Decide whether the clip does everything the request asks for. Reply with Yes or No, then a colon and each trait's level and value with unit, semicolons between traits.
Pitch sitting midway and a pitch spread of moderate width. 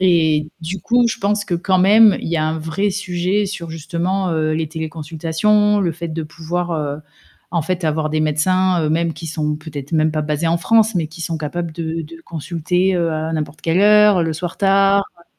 Yes: medium, 165 Hz; average, 3.0 semitones